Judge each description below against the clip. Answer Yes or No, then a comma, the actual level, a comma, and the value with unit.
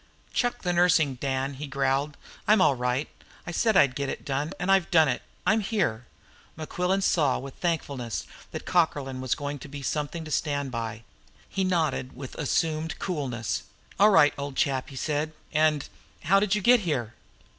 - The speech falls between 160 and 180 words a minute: Yes, average, 175 wpm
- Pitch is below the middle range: No, medium, 145 Hz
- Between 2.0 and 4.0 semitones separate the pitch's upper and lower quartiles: No, average, 4.7 semitones